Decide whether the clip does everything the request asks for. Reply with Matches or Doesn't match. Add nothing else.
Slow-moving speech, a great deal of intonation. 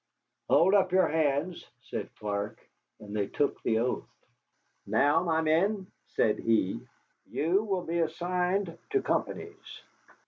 Matches